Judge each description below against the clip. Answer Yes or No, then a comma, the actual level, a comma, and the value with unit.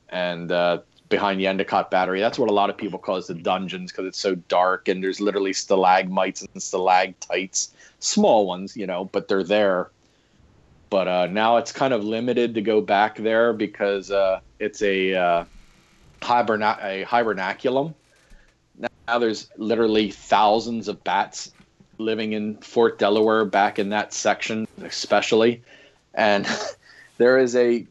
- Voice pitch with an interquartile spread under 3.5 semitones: Yes, average, 2.9 semitones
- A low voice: Yes, low, 105 Hz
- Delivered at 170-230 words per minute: No, average, 155 wpm